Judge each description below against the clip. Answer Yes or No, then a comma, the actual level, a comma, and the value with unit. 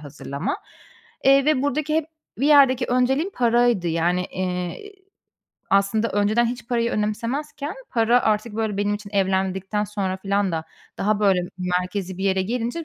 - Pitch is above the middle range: Yes, high, 210 Hz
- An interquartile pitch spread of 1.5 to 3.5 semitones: No, average, 4.6 semitones